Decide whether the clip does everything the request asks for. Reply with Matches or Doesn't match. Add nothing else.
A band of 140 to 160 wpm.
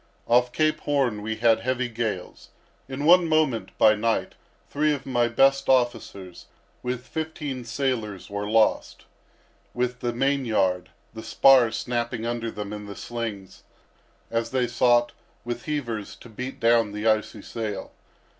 Matches